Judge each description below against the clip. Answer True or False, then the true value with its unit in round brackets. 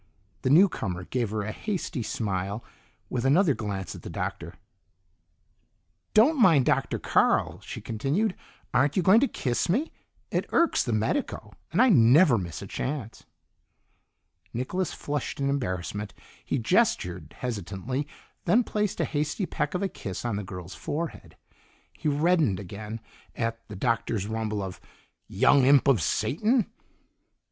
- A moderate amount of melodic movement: False (8.2 semitones)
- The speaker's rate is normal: True (145 wpm)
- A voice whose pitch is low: True (125 Hz)